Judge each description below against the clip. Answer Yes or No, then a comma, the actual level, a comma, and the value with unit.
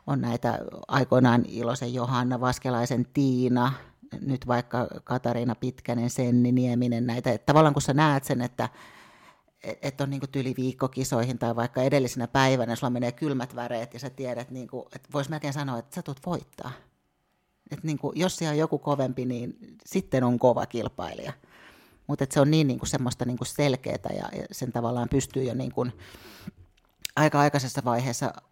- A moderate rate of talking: No, fast, 165 wpm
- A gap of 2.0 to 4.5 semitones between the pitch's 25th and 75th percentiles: Yes, narrow, 2.6 semitones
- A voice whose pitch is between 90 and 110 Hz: No, low, 125 Hz